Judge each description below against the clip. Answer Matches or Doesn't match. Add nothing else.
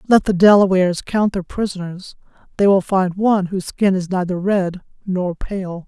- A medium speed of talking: Matches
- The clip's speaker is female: Matches